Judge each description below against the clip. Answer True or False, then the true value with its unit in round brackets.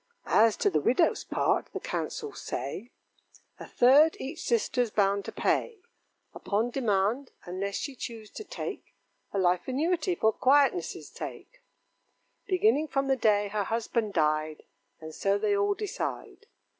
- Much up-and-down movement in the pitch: True (6.3 semitones)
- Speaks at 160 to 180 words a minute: False (145 wpm)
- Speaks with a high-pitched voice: True (230 Hz)